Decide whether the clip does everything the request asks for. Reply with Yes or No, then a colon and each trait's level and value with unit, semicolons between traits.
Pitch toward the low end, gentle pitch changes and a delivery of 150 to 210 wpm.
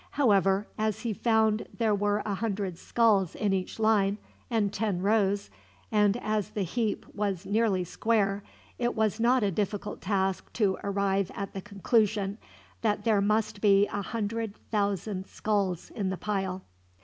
No: high, 205 Hz; narrow, 1.8 semitones; average, 155 wpm